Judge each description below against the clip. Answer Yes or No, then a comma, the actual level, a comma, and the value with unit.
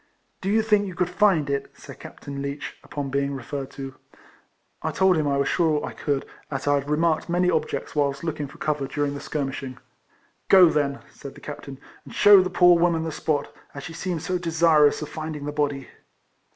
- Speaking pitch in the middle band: Yes, medium, 150 Hz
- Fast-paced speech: Yes, fast, 215 wpm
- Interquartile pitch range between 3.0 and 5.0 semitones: Yes, average, 3.4 semitones